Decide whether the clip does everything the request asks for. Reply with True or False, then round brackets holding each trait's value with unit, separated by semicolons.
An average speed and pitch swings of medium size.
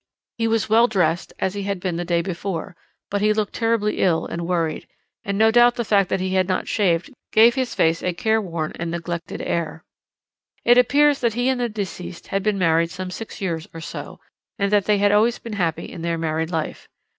False (215 wpm; 4.5 semitones)